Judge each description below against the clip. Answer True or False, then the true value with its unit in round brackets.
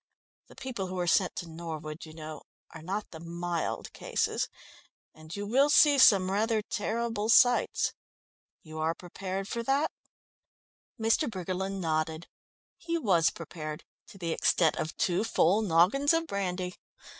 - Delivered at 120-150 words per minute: True (145 wpm)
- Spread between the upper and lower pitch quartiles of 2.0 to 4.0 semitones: False (5.2 semitones)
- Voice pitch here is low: False (185 Hz)